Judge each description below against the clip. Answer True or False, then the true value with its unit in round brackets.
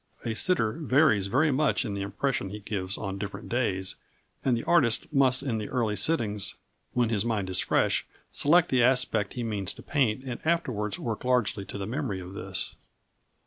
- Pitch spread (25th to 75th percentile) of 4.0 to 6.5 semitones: True (4.6 semitones)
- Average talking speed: True (185 wpm)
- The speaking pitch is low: True (115 Hz)